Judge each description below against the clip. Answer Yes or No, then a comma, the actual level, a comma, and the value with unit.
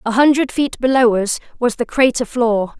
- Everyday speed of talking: Yes, average, 195 wpm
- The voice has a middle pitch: No, high, 240 Hz